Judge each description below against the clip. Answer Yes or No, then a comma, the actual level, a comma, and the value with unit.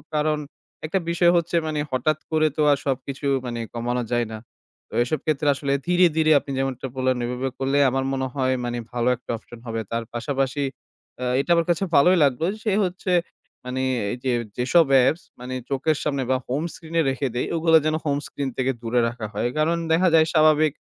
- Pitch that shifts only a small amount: No, average, 3.7 semitones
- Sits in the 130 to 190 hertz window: Yes, medium, 140 Hz